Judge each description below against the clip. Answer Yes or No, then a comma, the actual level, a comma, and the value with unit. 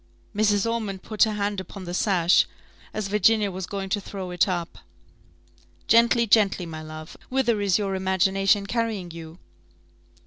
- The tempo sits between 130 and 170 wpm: Yes, average, 150 wpm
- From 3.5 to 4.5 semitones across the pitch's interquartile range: No, average, 2.7 semitones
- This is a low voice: No, high, 195 Hz